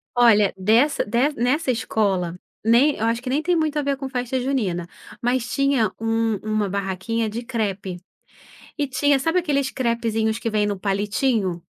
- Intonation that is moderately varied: Yes, average, 4.3 semitones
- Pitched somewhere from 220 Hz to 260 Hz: Yes, high, 230 Hz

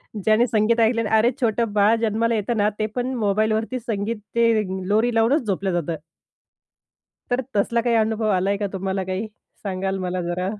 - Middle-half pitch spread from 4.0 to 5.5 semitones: No, average, 2.8 semitones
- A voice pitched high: Yes, high, 215 Hz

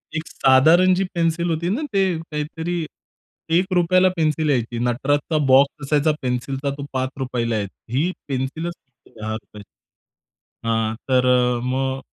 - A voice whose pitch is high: No, medium, 140 Hz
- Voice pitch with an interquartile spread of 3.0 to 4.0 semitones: No, average, 4.5 semitones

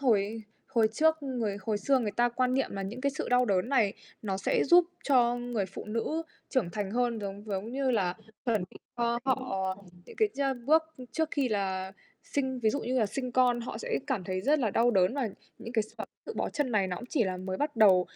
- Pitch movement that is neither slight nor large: Yes, average, 4.6 semitones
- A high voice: Yes, high, 235 Hz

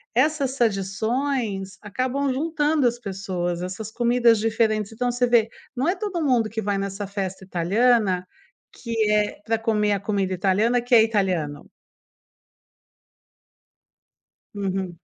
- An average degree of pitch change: Yes, average, 4.0 semitones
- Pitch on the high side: Yes, high, 220 Hz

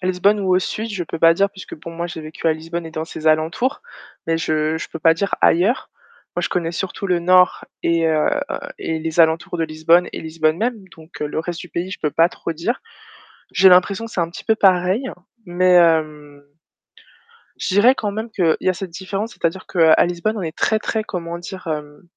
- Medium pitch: Yes, medium, 170 Hz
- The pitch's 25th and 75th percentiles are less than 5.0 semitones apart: Yes, average, 2.9 semitones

